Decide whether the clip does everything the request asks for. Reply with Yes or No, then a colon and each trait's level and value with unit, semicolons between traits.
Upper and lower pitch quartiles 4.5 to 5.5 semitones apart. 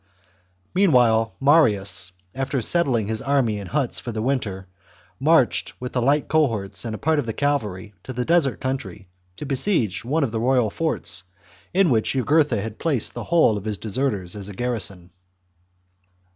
Yes: average, 5.1 semitones